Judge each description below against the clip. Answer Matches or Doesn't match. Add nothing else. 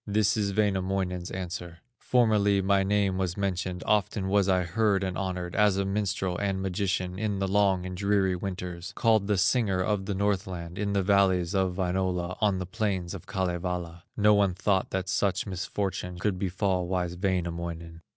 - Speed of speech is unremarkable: Matches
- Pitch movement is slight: Matches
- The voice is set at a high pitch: Doesn't match